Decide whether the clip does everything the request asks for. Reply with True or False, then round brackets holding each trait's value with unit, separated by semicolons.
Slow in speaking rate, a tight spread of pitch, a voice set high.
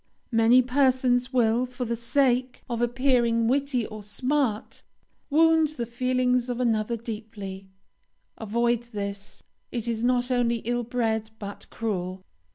True (130 wpm; 2.3 semitones; 240 Hz)